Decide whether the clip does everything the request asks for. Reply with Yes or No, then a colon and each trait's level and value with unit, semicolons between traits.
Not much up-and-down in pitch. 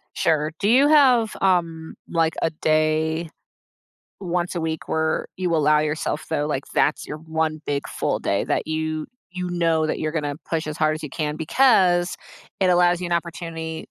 Yes: narrow, 2.1 semitones